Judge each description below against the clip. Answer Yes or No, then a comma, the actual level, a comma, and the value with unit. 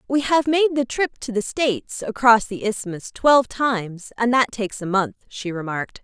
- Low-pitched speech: No, high, 230 Hz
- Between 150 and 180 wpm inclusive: No, average, 200 wpm